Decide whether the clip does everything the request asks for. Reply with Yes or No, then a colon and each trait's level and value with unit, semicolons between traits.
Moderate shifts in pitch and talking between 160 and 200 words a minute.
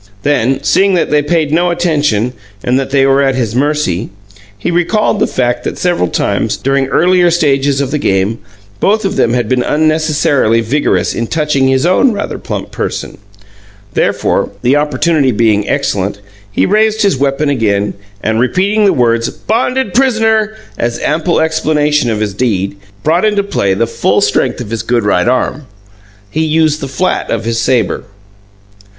No: wide, 6.4 semitones; average, 170 wpm